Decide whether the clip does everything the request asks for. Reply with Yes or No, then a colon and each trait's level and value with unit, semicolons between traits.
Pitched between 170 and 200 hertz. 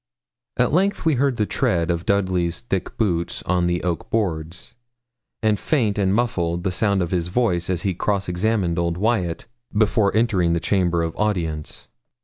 No: very low, 95 Hz